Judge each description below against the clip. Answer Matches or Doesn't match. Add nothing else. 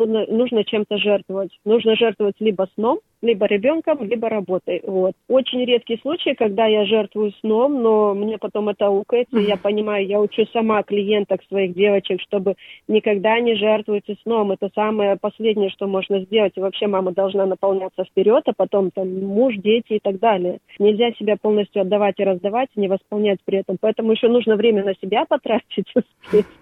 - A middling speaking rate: Doesn't match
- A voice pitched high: Matches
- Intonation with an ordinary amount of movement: Doesn't match